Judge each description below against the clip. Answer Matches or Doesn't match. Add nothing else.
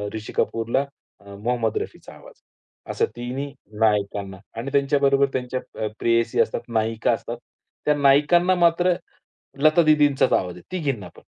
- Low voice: Matches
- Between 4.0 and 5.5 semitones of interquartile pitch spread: Matches